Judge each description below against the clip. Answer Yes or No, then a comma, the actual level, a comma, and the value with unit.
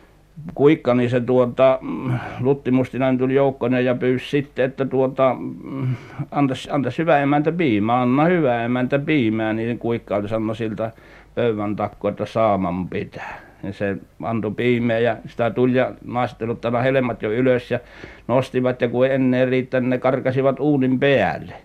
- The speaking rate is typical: Yes, average, 145 wpm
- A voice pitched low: Yes, low, 125 Hz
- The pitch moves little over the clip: Yes, narrow, 2.2 semitones